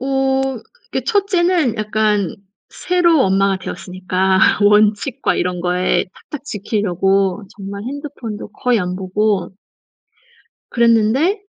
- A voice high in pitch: Yes, high, 215 Hz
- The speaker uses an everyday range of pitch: No, wide, 5.8 semitones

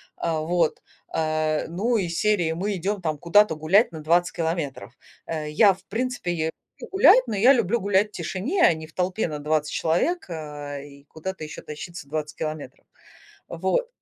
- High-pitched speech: No, medium, 170 Hz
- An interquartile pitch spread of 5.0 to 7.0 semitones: No, average, 4.5 semitones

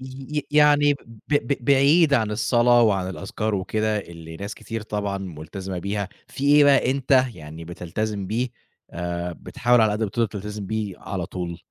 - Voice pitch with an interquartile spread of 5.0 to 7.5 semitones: Yes, wide, 5.5 semitones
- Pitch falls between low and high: No, low, 105 Hz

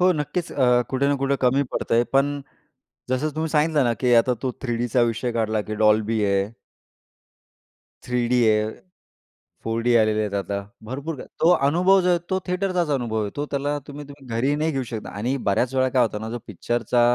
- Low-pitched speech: Yes, low, 125 Hz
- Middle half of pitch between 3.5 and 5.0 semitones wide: Yes, average, 4.2 semitones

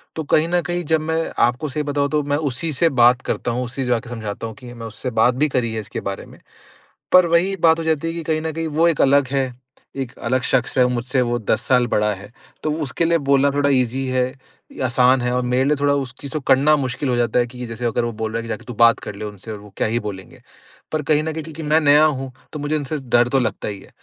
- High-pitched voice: No, low, 130 Hz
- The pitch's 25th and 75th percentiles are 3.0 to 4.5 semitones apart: Yes, average, 4.2 semitones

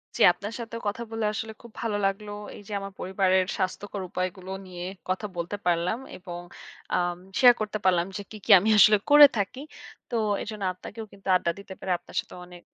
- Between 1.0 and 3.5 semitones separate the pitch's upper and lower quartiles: Yes, average, 2.9 semitones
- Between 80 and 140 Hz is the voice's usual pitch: No, high, 195 Hz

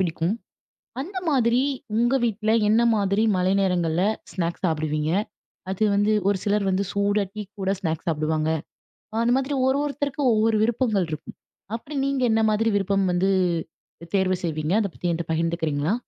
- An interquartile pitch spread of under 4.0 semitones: No, average, 5.1 semitones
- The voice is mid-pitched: No, high, 200 Hz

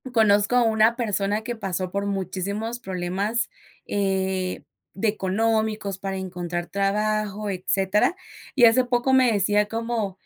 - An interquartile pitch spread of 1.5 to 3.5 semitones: Yes, average, 2.9 semitones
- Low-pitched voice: No, high, 205 Hz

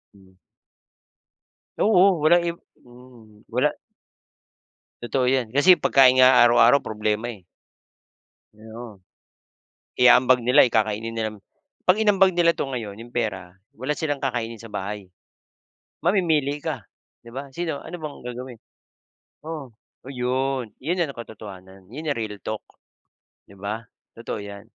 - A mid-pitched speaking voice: No, low, 125 Hz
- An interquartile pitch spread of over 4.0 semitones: Yes, average, 4.6 semitones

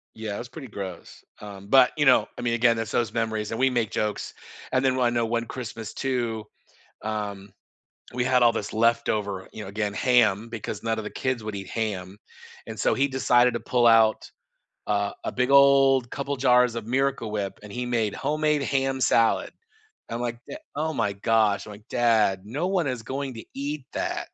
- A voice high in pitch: No, low, 115 Hz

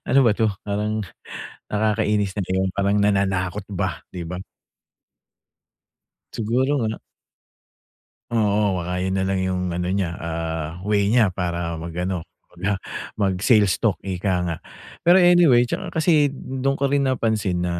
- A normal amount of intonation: Yes, average, 3.9 semitones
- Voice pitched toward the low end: Yes, low, 100 Hz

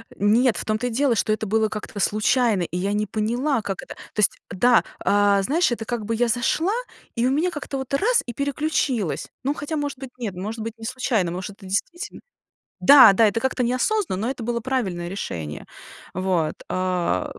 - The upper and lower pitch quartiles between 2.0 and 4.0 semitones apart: No, average, 4.6 semitones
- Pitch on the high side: Yes, high, 225 Hz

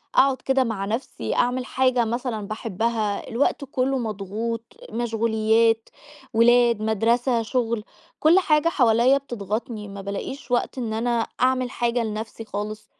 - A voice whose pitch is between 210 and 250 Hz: Yes, high, 230 Hz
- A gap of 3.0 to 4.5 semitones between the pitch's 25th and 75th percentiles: No, narrow, 2.4 semitones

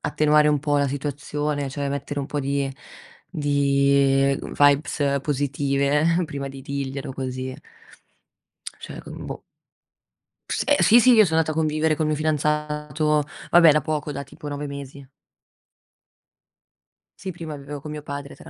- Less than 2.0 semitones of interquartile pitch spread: Yes, narrow, 1.5 semitones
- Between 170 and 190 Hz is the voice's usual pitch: No, medium, 145 Hz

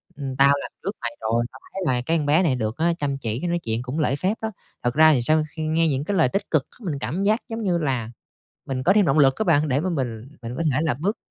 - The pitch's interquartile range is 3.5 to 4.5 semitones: No, average, 5.0 semitones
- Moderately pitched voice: Yes, medium, 150 Hz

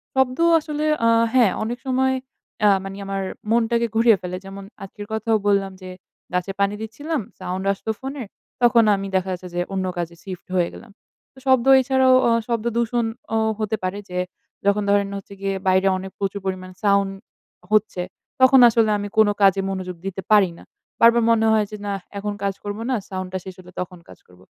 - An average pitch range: Yes, average, 3.5 semitones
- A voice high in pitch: Yes, high, 205 Hz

